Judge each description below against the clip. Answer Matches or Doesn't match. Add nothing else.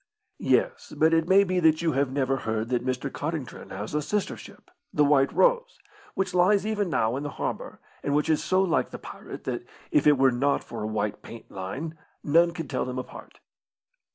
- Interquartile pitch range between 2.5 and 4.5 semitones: Doesn't match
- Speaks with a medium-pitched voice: Matches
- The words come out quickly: Matches